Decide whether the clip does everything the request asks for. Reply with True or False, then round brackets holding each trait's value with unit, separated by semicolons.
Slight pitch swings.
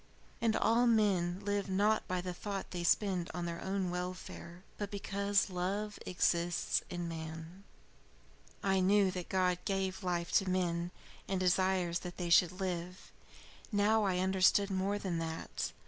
True (2.2 semitones)